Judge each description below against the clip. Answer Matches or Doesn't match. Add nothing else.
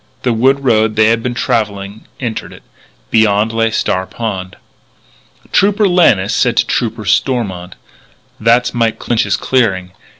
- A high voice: Doesn't match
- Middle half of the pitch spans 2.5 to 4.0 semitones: Matches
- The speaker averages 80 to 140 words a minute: Matches